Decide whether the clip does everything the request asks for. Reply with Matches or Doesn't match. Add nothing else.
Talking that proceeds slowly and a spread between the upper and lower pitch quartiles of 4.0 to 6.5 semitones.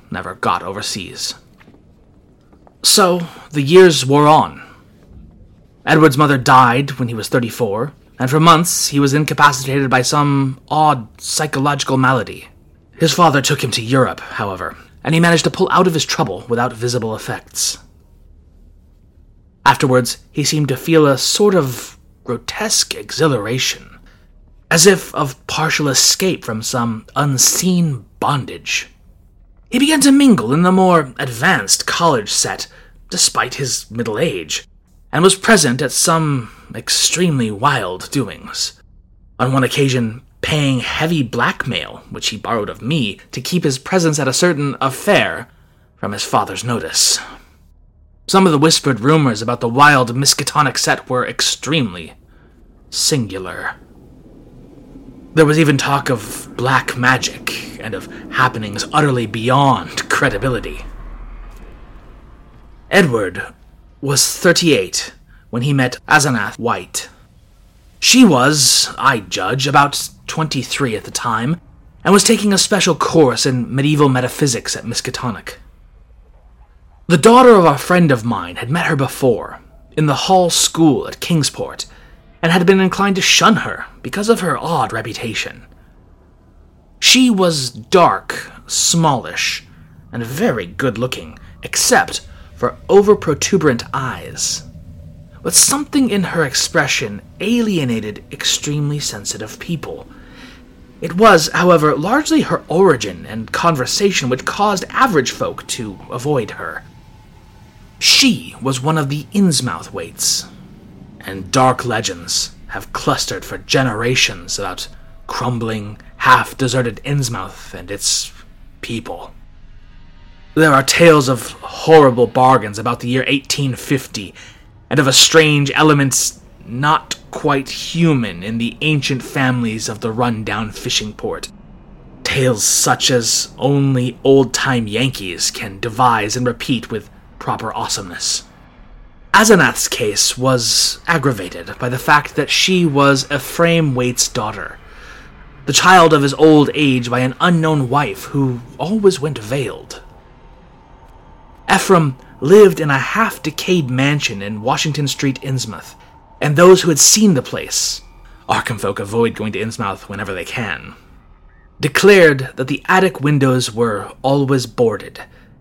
Matches